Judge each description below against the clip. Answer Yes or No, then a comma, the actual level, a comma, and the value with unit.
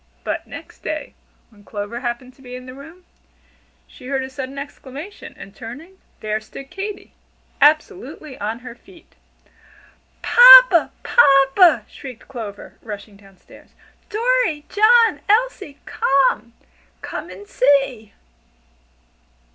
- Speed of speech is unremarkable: No, slow, 120 wpm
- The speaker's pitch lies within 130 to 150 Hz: No, very high, 270 Hz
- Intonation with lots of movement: Yes, wide, 7.4 semitones